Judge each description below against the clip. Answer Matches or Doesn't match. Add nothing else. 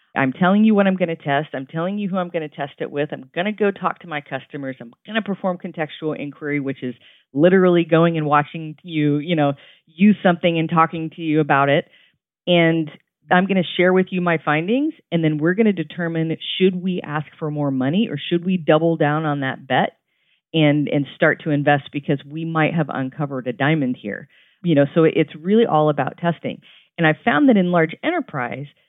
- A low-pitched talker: Doesn't match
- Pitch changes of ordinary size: Matches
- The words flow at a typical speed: Doesn't match